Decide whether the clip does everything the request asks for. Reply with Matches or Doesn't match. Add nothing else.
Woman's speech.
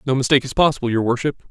Doesn't match